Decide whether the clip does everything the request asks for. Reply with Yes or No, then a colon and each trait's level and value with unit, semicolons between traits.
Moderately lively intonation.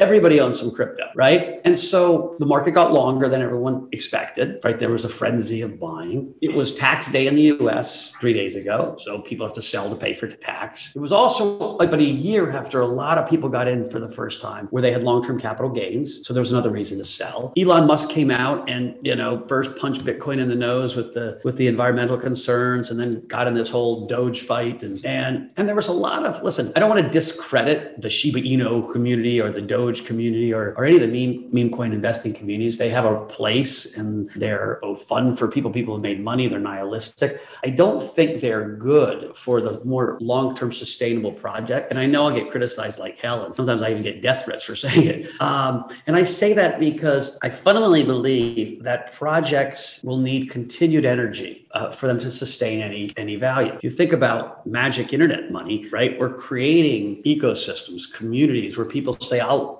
Yes: average, 4.1 semitones